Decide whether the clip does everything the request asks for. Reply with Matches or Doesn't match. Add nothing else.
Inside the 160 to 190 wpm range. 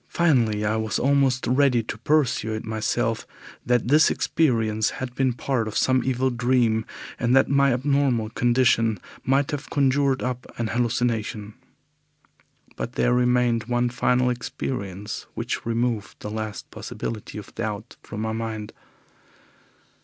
Doesn't match